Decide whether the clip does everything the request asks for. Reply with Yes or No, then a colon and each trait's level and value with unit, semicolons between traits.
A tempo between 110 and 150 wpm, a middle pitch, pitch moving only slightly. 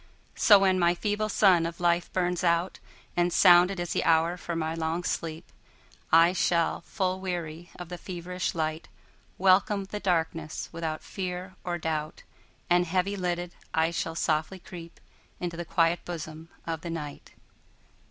Yes: average, 140 wpm; medium, 175 Hz; narrow, 1.8 semitones